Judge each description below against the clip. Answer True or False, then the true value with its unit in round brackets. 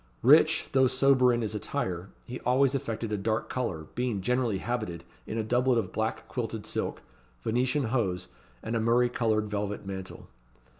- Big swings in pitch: False (3.3 semitones)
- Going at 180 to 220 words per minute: False (165 wpm)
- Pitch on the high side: False (115 Hz)